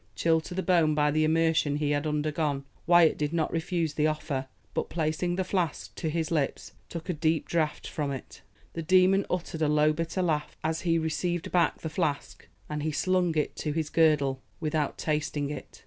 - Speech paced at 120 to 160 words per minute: No, average, 195 wpm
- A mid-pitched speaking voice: Yes, medium, 155 Hz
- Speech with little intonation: Yes, narrow, 1.9 semitones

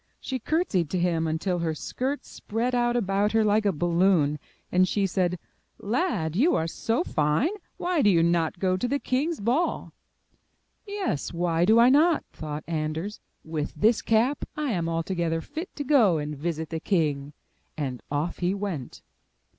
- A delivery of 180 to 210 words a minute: No, average, 170 wpm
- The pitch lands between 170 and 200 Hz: Yes, medium, 185 Hz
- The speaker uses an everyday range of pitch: No, wide, 6.8 semitones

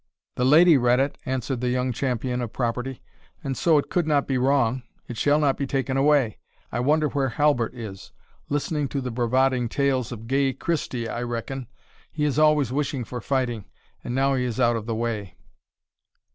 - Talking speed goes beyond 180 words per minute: Yes, average, 190 wpm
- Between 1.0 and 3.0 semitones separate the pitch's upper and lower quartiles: Yes, narrow, 2.6 semitones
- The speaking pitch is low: Yes, low, 130 Hz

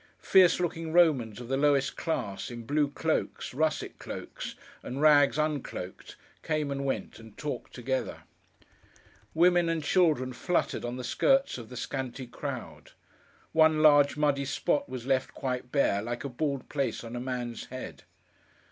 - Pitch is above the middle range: No, medium, 140 Hz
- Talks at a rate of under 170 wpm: Yes, average, 155 wpm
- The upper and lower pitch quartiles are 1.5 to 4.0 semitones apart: Yes, average, 3.7 semitones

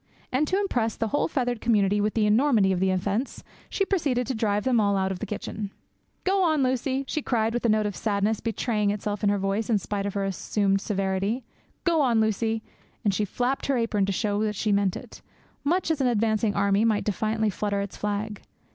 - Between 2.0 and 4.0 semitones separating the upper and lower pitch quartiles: Yes, average, 3.3 semitones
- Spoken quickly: Yes, fast, 215 wpm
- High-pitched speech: Yes, high, 215 Hz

